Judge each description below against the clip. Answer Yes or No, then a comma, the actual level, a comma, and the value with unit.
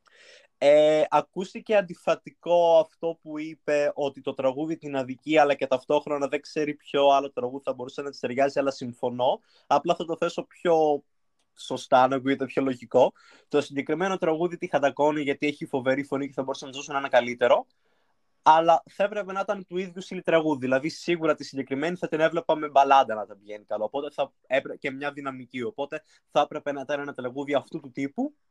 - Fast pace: Yes, fast, 185 wpm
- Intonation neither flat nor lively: Yes, average, 3.1 semitones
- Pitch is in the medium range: Yes, medium, 145 Hz